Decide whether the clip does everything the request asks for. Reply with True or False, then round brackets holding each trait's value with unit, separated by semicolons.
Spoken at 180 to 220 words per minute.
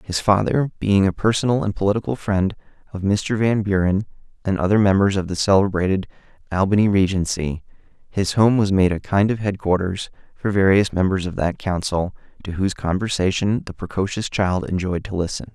False (165 wpm)